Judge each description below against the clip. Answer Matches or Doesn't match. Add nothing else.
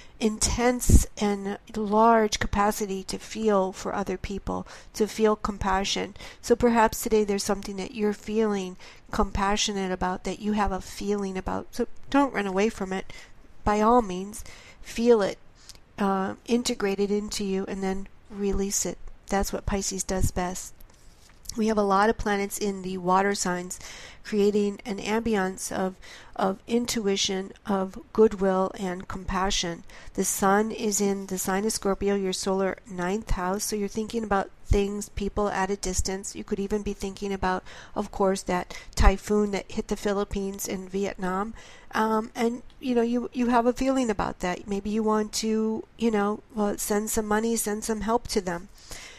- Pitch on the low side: Doesn't match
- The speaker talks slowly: Doesn't match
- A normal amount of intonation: Doesn't match